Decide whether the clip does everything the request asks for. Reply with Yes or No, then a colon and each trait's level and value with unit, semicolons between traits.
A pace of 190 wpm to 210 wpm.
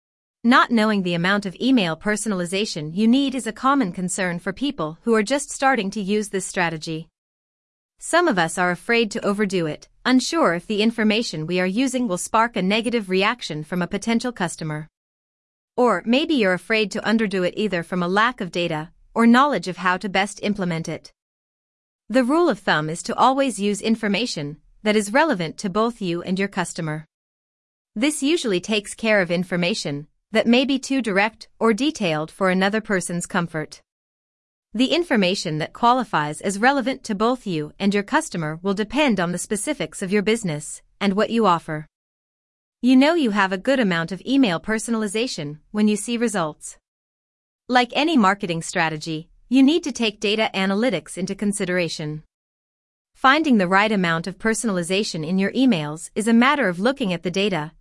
No: average, 175 wpm